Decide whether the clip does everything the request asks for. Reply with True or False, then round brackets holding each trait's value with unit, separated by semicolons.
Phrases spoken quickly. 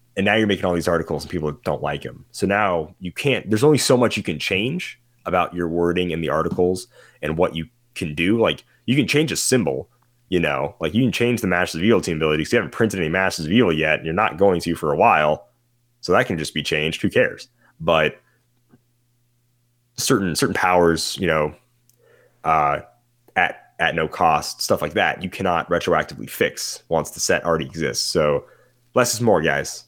True (210 wpm)